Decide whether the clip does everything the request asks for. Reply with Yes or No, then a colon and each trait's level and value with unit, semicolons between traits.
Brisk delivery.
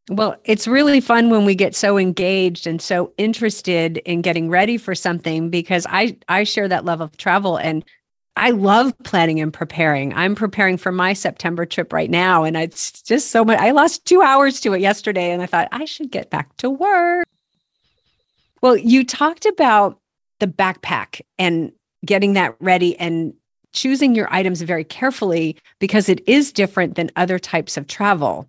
No: average, 180 wpm